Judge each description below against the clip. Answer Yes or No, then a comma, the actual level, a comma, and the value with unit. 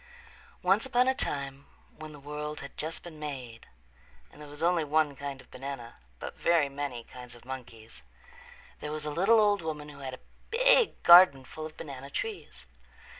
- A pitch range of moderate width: Yes, average, 3.6 semitones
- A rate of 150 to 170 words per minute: No, average, 180 wpm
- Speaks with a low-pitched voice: No, medium, 150 Hz